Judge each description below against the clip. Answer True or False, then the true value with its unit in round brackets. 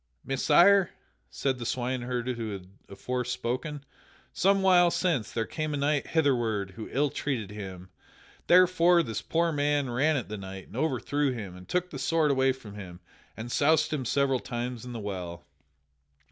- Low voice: True (130 Hz)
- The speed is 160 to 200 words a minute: True (170 wpm)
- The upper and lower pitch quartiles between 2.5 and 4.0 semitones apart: False (5.3 semitones)